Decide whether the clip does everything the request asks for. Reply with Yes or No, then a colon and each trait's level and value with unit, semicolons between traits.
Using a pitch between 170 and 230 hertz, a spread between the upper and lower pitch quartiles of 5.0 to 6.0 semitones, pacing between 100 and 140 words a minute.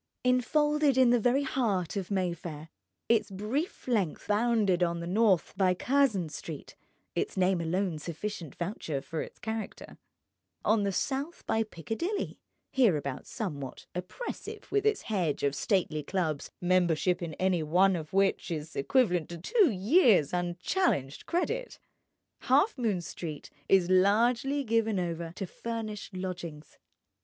Yes: high, 190 Hz; wide, 5.5 semitones; slow, 135 wpm